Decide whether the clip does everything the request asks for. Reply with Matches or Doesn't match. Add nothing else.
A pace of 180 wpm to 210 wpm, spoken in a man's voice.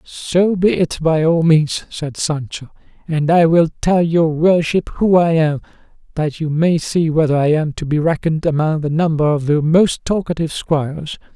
Matches